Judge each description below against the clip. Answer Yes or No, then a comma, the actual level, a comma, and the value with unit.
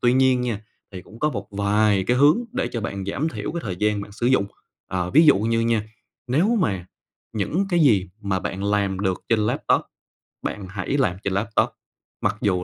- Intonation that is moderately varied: Yes, average, 4.4 semitones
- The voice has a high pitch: No, low, 105 Hz